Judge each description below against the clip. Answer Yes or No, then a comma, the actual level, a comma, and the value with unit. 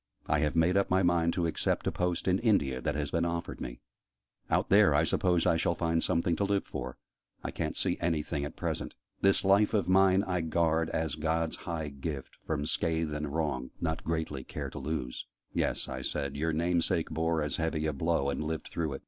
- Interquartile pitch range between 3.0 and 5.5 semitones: No, narrow, 2.4 semitones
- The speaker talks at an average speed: No, fast, 215 wpm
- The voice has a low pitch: Yes, very low, 80 Hz